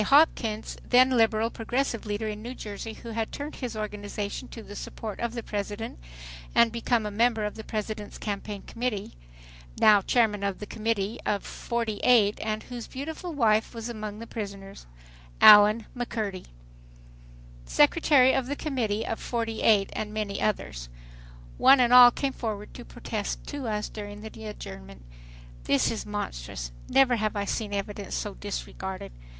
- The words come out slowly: No, average, 160 wpm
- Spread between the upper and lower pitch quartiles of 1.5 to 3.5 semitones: Yes, narrow, 2.5 semitones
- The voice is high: Yes, high, 215 Hz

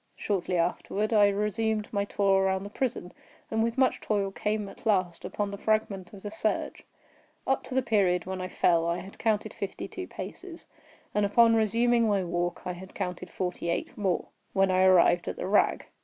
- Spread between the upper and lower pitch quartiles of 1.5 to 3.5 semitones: Yes, average, 2.9 semitones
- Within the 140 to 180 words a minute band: No, average, 190 wpm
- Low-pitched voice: No, high, 200 Hz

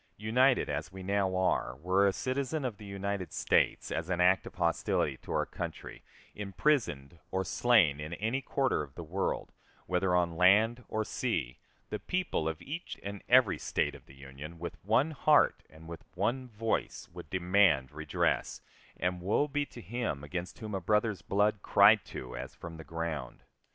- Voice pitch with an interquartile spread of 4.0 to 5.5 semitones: Yes, average, 5.1 semitones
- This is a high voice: No, very low, 95 Hz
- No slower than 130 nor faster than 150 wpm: No, average, 175 wpm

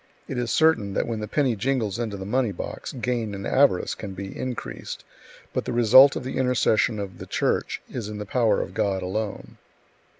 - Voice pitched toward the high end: No, low, 110 Hz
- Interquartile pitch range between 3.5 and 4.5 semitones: Yes, average, 3.9 semitones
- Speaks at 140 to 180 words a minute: No, average, 200 wpm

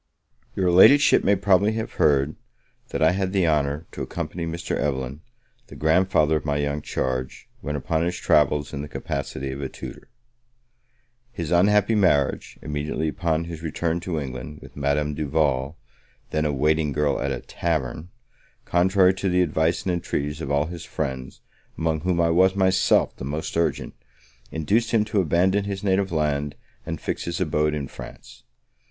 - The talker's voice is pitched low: Yes, very low, 80 Hz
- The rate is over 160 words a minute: Yes, average, 170 wpm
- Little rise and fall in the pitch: No, average, 3.8 semitones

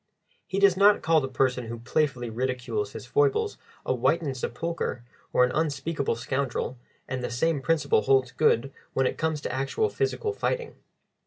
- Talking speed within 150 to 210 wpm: Yes, average, 165 wpm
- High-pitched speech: No, medium, 140 Hz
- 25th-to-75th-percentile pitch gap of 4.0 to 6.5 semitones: Yes, average, 5.0 semitones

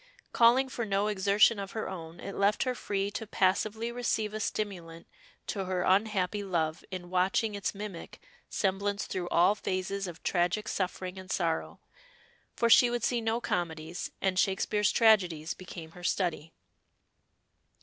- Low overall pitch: No, high, 195 Hz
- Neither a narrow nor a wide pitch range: Yes, average, 3.0 semitones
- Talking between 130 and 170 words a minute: Yes, average, 150 wpm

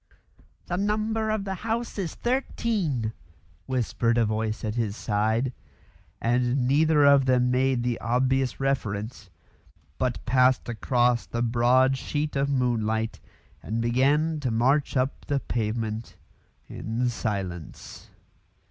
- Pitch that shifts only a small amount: No, average, 3.6 semitones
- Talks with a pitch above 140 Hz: No, low, 125 Hz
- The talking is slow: Yes, slow, 120 wpm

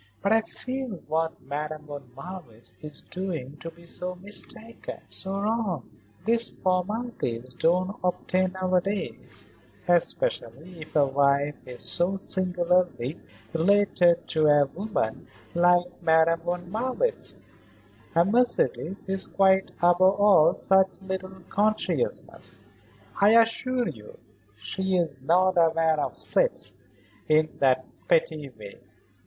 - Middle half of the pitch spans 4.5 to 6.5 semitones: No, average, 4.0 semitones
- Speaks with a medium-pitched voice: Yes, medium, 180 Hz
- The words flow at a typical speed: No, slow, 115 wpm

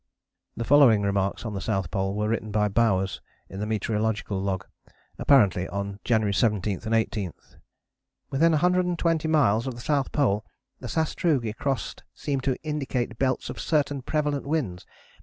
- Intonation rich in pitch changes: Yes, wide, 6.0 semitones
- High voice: No, low, 115 Hz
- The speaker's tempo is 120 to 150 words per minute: No, average, 160 wpm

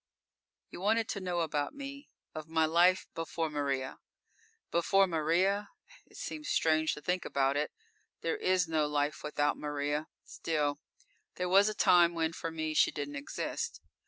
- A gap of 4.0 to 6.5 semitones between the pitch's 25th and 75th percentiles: No, average, 3.6 semitones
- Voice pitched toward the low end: No, medium, 160 Hz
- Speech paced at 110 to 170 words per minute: Yes, average, 160 wpm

